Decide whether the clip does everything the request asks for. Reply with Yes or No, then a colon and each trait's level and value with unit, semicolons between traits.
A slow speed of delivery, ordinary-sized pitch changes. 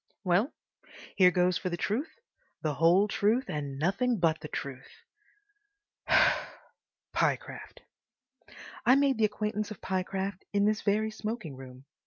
Yes: slow, 130 wpm; average, 4.5 semitones